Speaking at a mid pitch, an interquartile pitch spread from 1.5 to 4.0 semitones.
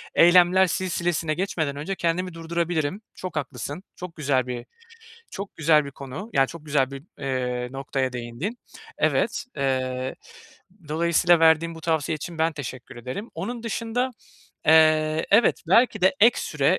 No: medium, 160 Hz; average, 4.7 semitones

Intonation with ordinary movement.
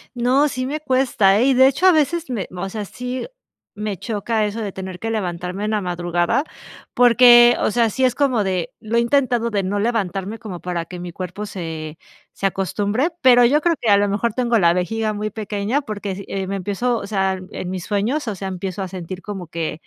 Yes: average, 4.3 semitones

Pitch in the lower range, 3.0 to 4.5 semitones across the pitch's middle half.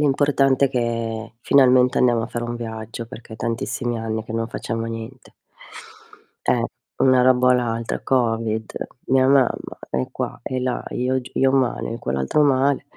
No: low, 120 Hz; narrow, 2.4 semitones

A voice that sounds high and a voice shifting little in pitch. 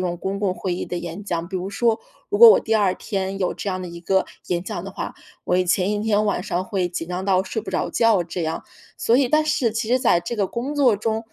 No: high, 195 Hz; average, 3.7 semitones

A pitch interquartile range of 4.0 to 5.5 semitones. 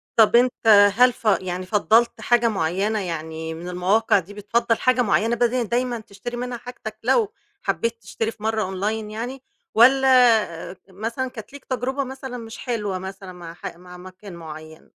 Yes: average, 4.5 semitones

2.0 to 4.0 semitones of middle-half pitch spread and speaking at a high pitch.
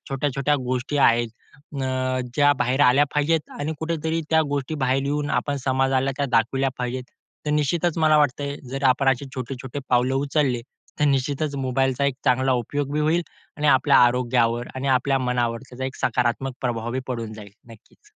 No: narrow, 2.5 semitones; low, 135 Hz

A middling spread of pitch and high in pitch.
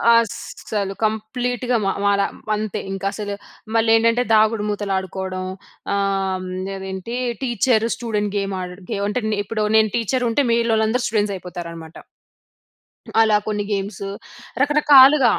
Yes: average, 3.0 semitones; high, 210 Hz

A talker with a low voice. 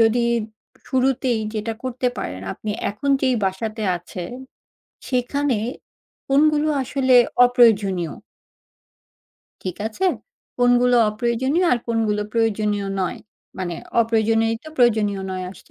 No: high, 230 Hz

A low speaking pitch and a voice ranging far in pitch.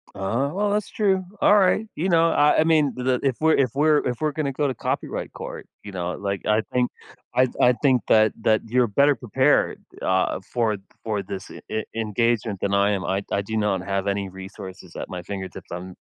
Yes: low, 115 Hz; wide, 6.3 semitones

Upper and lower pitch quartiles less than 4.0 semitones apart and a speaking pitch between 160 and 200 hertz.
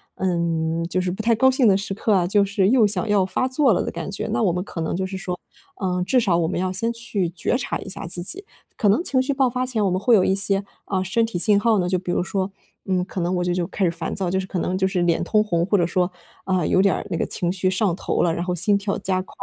Yes: average, 2.8 semitones; high, 190 Hz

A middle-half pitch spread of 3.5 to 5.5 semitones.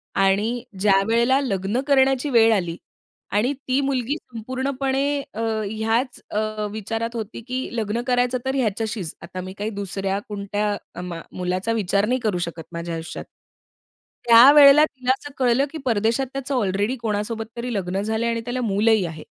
Yes: average, 4.2 semitones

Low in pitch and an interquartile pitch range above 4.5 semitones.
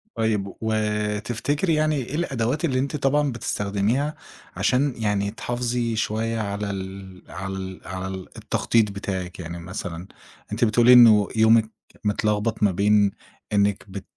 No: low, 105 Hz; average, 3.6 semitones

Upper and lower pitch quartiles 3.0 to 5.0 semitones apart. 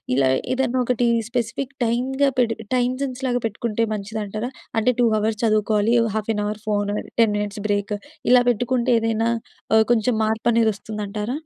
No: narrow, 2.6 semitones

